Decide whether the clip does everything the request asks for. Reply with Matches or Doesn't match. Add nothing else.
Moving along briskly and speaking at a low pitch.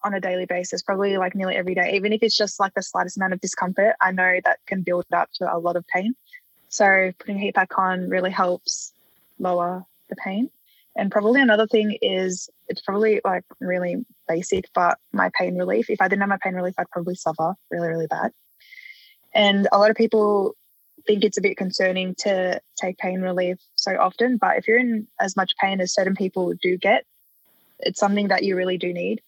Doesn't match